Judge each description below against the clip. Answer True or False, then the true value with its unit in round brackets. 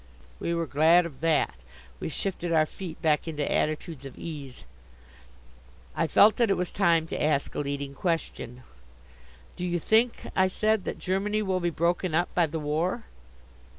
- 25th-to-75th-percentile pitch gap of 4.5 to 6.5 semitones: False (3.4 semitones)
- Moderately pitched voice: True (170 Hz)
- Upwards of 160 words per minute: True (170 wpm)